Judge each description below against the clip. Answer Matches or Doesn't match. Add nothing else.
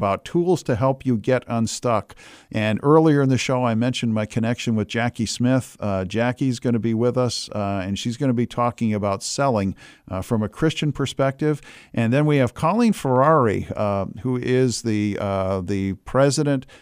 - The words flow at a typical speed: Matches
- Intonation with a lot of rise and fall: Doesn't match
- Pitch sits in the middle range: Doesn't match